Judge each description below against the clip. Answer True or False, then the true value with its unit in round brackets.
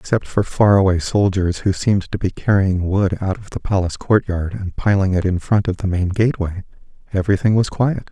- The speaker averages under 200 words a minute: False (205 wpm)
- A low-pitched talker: True (95 Hz)